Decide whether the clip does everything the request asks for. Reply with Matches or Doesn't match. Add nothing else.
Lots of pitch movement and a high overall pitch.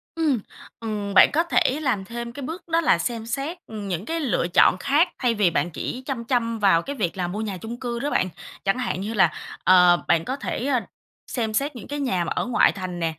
Matches